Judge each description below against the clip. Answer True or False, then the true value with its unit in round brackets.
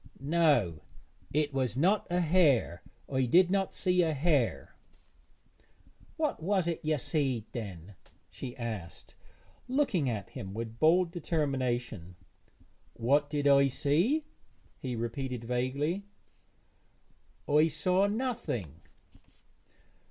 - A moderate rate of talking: False (105 wpm)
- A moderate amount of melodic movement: False (6.4 semitones)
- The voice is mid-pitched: True (145 Hz)